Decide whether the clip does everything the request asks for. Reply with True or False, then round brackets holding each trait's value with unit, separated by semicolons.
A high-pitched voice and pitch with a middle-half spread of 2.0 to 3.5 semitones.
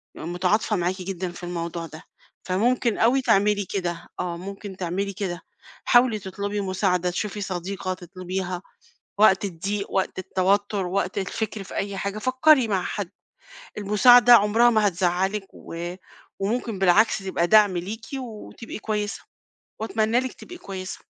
True (195 Hz; 2.8 semitones)